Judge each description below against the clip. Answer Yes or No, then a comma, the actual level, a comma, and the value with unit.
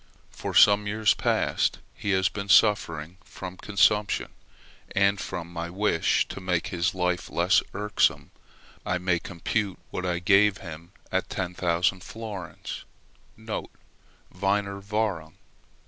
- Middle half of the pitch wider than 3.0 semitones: No, average, 2.7 semitones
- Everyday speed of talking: No, slow, 120 wpm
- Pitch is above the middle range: No, very low, 95 Hz